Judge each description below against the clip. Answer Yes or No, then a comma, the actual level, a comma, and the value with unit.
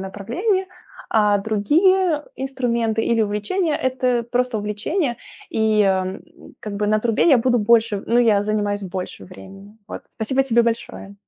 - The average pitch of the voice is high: Yes, high, 225 Hz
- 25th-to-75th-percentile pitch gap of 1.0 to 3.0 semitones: No, average, 3.6 semitones